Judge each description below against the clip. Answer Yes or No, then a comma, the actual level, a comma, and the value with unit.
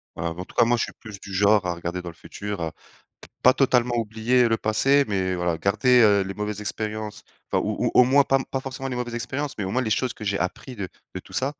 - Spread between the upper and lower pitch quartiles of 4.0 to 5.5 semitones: Yes, average, 4.4 semitones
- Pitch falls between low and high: No, low, 110 Hz